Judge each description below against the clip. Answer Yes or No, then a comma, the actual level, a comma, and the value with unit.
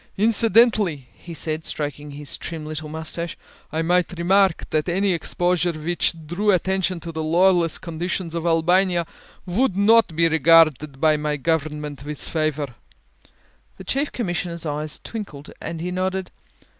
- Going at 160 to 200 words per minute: No, average, 145 wpm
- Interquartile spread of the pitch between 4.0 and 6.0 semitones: No, average, 3.1 semitones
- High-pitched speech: No, medium, 170 Hz